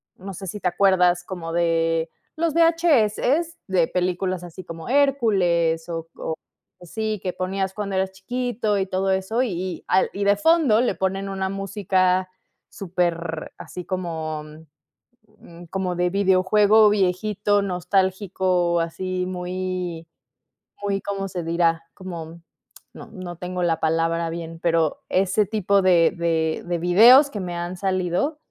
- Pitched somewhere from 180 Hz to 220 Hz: Yes, medium, 185 Hz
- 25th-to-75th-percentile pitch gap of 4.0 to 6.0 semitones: No, narrow, 2.6 semitones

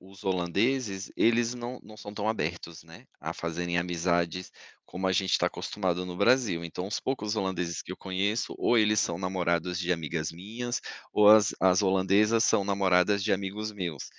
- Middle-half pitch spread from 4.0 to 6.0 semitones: No, average, 3.2 semitones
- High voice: No, very low, 95 Hz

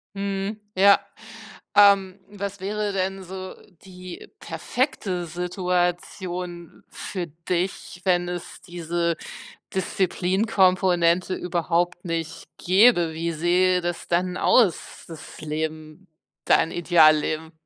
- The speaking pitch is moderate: Yes, medium, 180 Hz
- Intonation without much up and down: Yes, narrow, 2.0 semitones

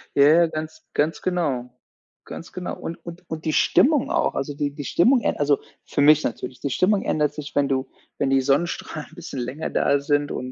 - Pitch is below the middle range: No, medium, 150 Hz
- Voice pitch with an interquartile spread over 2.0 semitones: Yes, average, 2.8 semitones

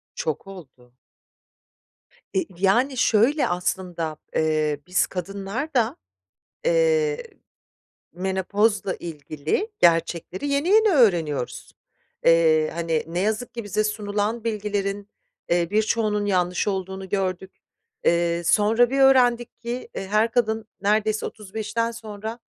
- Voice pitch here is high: Yes, high, 205 Hz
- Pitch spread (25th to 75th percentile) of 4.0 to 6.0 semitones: Yes, average, 4.6 semitones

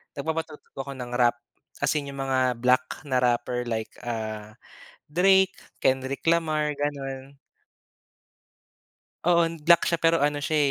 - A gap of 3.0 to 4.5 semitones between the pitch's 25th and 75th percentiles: Yes, average, 4.1 semitones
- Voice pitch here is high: No, medium, 140 Hz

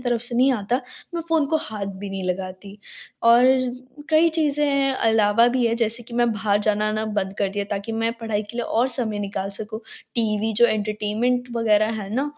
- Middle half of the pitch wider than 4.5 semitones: No, average, 2.9 semitones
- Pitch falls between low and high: No, high, 225 Hz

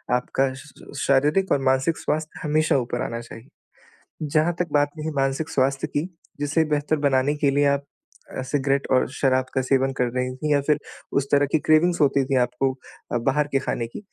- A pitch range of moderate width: No, narrow, 2.2 semitones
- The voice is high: No, medium, 140 Hz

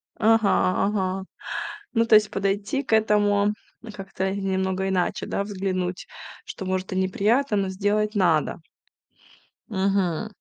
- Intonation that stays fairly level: Yes, narrow, 1.9 semitones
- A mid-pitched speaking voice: No, high, 195 Hz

